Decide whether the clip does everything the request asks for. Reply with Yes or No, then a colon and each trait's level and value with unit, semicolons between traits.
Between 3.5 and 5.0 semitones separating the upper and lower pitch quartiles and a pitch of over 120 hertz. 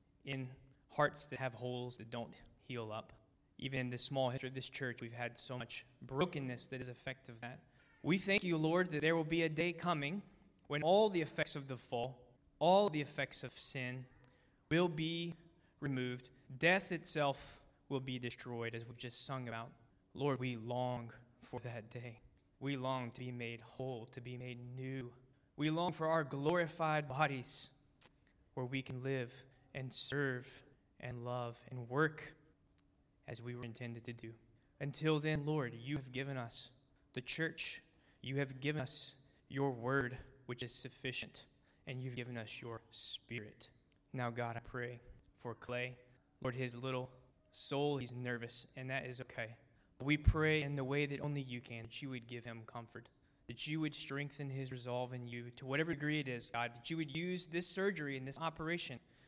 No: average, 3.1 semitones; low, 130 Hz